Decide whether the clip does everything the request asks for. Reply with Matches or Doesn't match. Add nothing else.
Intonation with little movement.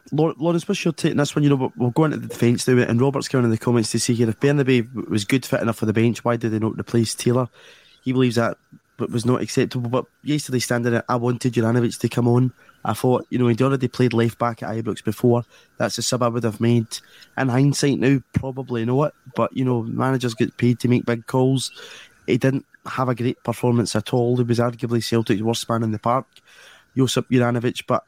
Matches